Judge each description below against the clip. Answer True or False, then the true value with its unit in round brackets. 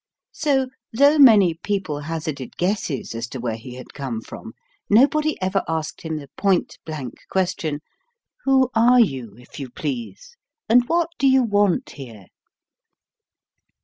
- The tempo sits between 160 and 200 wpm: False (145 wpm)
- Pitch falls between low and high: True (180 Hz)